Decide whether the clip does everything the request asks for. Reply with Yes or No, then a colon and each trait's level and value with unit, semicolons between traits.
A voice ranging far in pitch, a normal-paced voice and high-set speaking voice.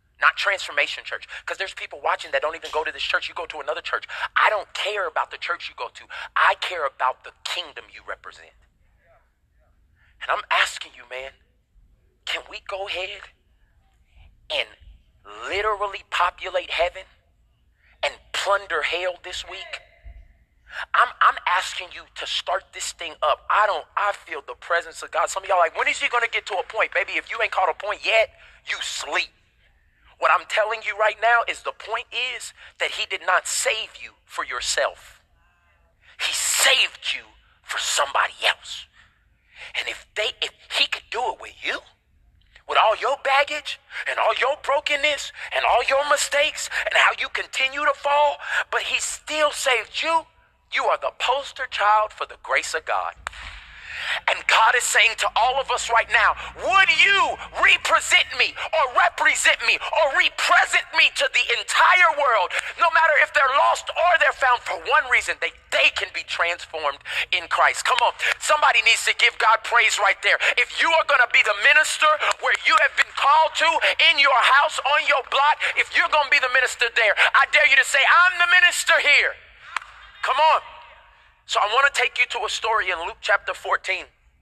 Yes: wide, 6.9 semitones; average, 185 wpm; very high, 265 Hz